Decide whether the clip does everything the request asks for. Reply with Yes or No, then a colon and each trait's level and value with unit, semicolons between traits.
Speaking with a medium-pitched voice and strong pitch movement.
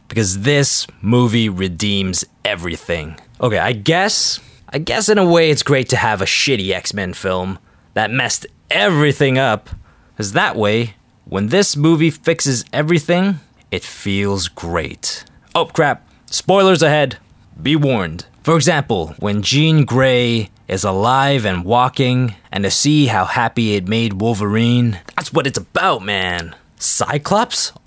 No: low, 120 Hz; wide, 6.6 semitones